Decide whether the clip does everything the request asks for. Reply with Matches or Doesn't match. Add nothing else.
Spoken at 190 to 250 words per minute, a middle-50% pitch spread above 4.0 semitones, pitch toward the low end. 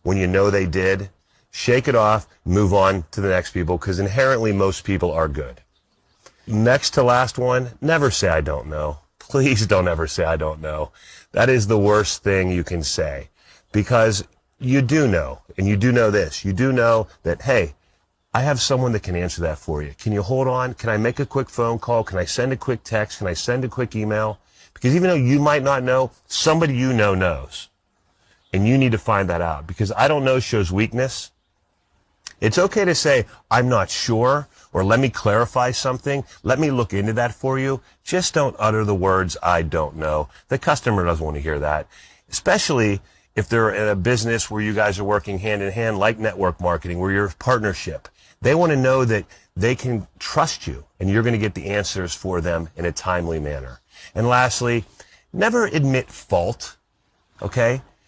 Matches